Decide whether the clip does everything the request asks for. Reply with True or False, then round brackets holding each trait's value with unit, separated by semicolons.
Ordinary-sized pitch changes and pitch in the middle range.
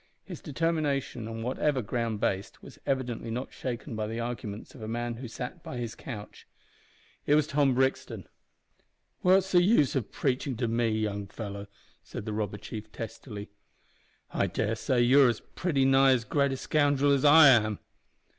False (3.8 semitones; 120 Hz)